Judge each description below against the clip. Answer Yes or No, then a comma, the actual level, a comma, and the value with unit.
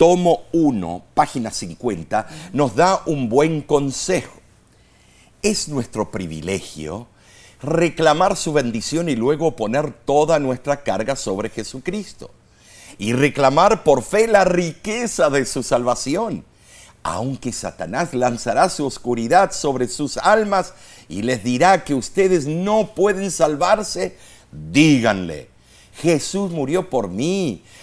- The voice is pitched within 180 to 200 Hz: No, medium, 145 Hz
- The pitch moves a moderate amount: No, wide, 6.9 semitones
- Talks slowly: Yes, slow, 115 wpm